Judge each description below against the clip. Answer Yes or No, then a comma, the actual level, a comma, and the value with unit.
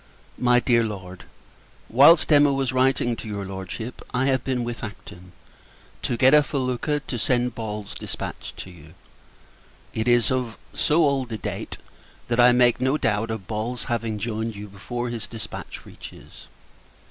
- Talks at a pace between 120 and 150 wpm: No, average, 160 wpm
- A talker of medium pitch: No, low, 120 Hz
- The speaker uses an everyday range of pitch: Yes, average, 3.2 semitones